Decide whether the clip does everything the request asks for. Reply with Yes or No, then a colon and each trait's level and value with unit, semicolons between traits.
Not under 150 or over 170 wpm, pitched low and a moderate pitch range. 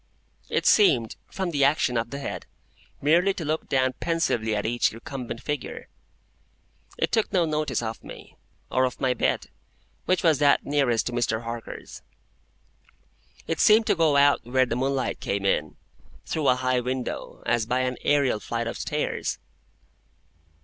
Yes: average, 160 wpm; low, 130 Hz; average, 4.4 semitones